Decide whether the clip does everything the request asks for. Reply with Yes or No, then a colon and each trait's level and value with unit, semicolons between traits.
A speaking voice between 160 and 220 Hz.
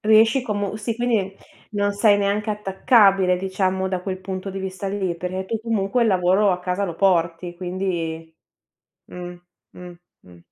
Yes: high, 190 Hz